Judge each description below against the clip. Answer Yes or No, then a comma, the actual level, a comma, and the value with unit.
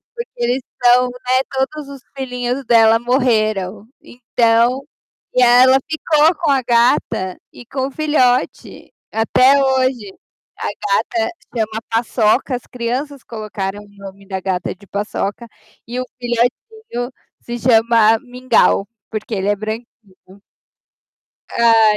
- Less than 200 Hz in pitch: No, high, 240 Hz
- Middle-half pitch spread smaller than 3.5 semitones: Yes, average, 2.9 semitones